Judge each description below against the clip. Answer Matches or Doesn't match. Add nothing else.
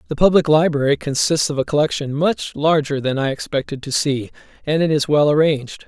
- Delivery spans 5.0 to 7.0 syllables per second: Matches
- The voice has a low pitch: Doesn't match